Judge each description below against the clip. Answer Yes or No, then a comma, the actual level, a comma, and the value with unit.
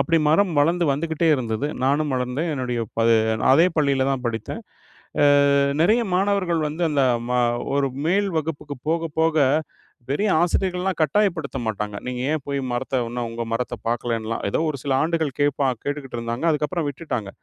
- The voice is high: No, medium, 145 Hz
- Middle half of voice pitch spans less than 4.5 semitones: No, average, 4.9 semitones